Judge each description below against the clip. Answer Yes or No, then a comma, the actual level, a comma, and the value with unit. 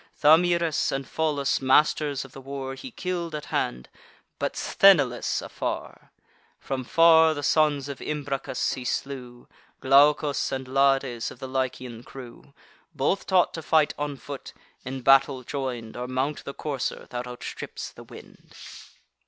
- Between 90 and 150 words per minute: Yes, average, 145 wpm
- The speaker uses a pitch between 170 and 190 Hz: No, low, 135 Hz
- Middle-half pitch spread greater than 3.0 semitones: No, narrow, 2.6 semitones